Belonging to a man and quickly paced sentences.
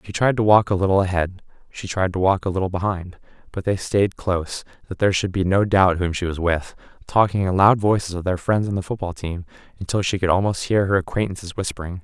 Yes: male; fast, 230 wpm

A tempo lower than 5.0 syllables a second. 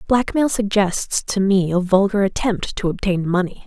Yes: 4.6 syllables/s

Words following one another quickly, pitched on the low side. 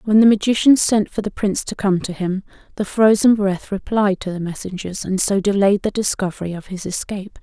No: fast, 210 wpm; high, 200 Hz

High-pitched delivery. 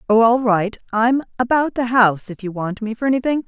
Yes: high, 230 Hz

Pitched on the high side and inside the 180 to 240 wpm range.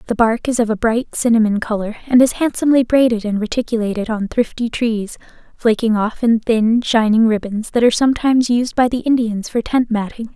Yes: high, 230 Hz; average, 190 wpm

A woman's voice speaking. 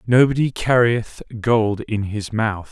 No: male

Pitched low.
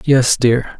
Yes: low, 125 Hz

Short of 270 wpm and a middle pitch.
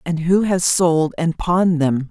Yes: average, 200 wpm; medium, 170 Hz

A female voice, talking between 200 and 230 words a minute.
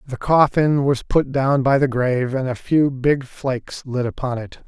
No: male; fast, 205 wpm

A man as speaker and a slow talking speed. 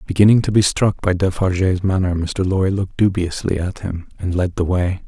No: male; average, 200 wpm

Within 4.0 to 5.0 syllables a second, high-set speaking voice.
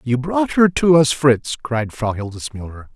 No: 4.3 syllables/s; low, 135 Hz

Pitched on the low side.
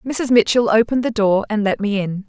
No: high, 220 Hz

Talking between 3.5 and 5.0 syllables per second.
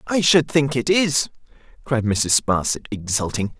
Yes: 4.4 syllables/s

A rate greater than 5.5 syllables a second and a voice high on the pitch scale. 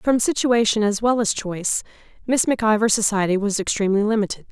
Yes: 6.0 syllables/s; high, 215 Hz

